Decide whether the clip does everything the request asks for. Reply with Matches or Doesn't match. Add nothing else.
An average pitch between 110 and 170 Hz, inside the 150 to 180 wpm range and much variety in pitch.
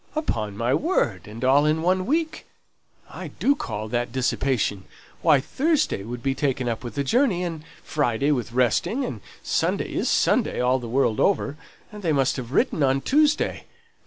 Matches